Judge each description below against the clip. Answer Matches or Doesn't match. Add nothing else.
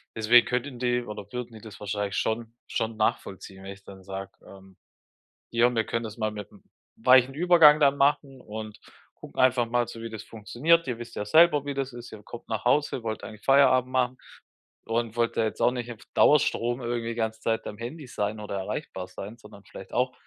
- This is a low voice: Matches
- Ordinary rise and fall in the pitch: Matches